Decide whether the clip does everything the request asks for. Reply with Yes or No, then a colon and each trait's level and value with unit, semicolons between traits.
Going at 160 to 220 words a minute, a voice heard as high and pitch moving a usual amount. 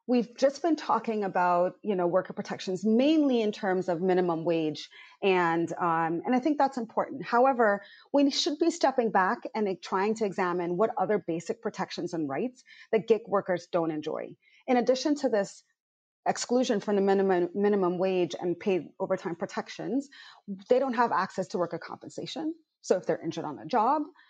No: average, 175 wpm; high, 205 Hz; wide, 5.8 semitones